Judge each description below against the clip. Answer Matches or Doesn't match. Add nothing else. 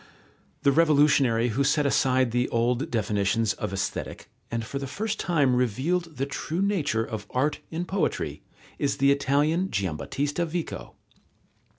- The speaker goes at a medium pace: Matches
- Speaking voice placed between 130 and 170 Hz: Matches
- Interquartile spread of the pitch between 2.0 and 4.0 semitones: Doesn't match